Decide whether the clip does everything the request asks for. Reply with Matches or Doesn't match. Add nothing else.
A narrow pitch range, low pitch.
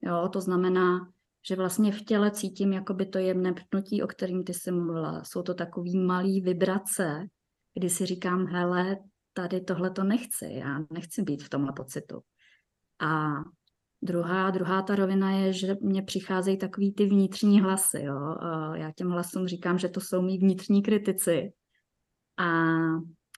Doesn't match